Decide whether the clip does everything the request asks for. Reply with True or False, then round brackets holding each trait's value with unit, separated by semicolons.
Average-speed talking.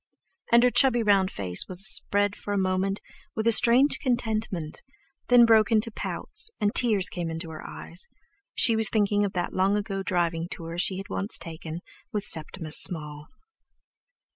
True (170 wpm)